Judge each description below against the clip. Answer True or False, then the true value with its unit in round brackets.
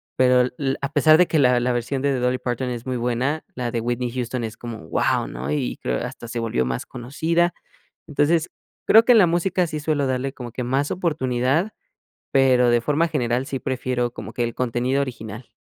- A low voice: True (125 Hz)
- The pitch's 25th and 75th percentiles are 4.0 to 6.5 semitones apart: False (3.2 semitones)